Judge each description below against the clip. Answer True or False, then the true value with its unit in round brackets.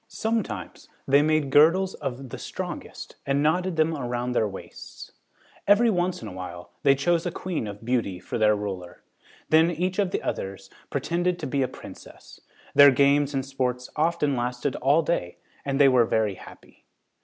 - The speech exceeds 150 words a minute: True (175 wpm)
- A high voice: False (140 Hz)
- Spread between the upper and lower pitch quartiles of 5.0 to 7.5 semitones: True (5.5 semitones)